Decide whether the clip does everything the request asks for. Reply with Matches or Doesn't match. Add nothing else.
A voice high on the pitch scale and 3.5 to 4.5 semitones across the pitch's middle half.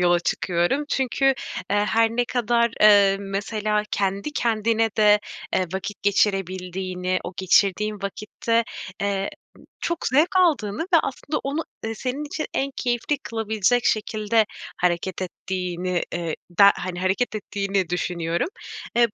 Matches